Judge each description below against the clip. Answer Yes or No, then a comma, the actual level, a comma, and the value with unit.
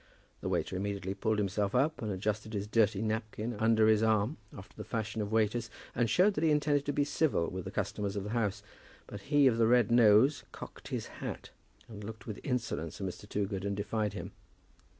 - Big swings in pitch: No, narrow, 2.6 semitones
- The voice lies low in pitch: Yes, low, 110 Hz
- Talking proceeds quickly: Yes, fast, 210 wpm